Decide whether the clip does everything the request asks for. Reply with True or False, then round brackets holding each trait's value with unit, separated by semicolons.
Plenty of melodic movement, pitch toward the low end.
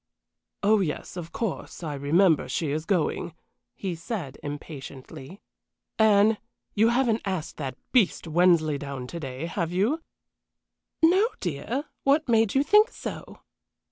False (6.7 semitones; 175 Hz)